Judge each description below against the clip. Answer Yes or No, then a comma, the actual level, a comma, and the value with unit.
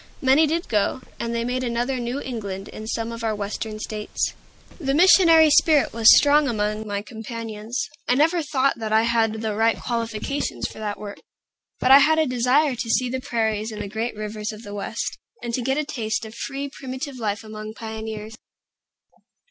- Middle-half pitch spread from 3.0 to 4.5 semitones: Yes, average, 3.5 semitones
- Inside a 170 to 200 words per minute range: Yes, average, 190 wpm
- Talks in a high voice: Yes, high, 230 Hz